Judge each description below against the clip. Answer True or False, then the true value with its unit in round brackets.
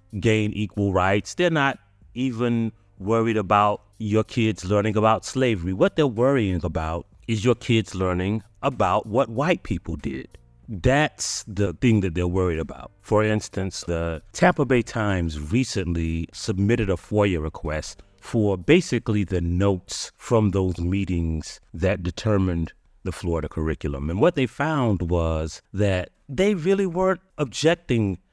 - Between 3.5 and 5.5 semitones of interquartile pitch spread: True (4.3 semitones)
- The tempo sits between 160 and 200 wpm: False (140 wpm)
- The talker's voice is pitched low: True (100 Hz)